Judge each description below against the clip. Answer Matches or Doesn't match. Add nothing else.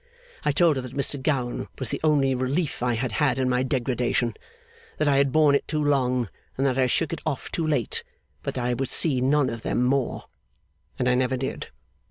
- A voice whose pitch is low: Matches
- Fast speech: Matches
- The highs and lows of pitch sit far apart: Doesn't match